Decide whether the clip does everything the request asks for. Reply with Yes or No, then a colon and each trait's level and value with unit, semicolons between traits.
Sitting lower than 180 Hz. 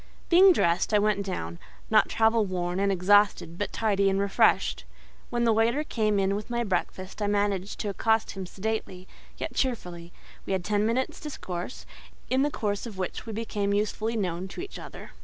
No: high, 205 Hz